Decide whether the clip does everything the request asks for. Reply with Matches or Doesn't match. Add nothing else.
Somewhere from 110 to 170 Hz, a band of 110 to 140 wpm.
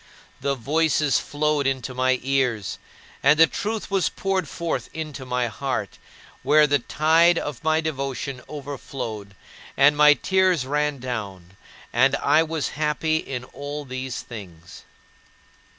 Matches